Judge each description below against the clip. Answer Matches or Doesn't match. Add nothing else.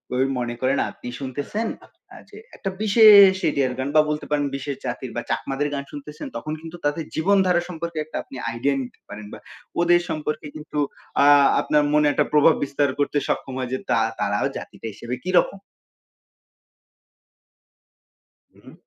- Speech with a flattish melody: Doesn't match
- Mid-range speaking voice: Matches